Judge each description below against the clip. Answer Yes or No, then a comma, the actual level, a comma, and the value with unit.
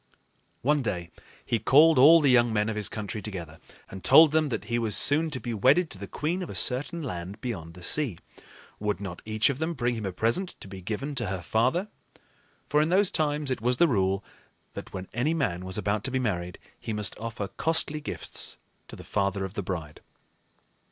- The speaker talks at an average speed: No, fast, 215 wpm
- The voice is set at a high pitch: No, low, 115 Hz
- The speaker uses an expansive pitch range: Yes, wide, 7.1 semitones